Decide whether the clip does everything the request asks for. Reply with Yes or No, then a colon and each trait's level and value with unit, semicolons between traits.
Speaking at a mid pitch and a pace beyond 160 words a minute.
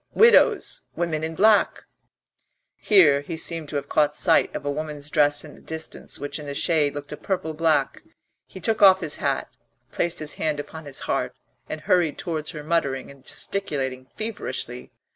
Yes: medium, 155 Hz; average, 180 wpm